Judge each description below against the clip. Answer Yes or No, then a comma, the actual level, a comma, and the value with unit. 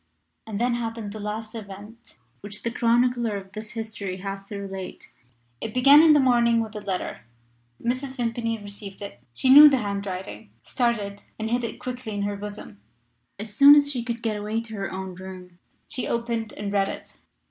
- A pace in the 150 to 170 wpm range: No, average, 190 wpm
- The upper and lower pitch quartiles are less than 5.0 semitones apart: Yes, average, 2.9 semitones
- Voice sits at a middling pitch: No, high, 220 Hz